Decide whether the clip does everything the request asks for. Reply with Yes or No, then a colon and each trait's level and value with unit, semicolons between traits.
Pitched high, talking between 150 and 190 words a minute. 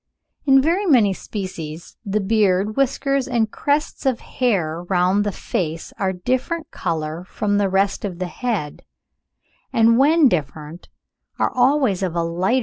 Yes: high, 205 Hz; average, 165 wpm